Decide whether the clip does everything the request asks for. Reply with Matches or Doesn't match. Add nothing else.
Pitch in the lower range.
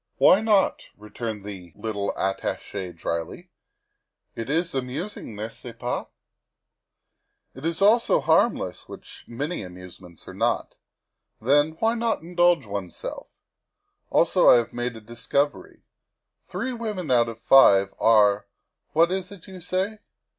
Matches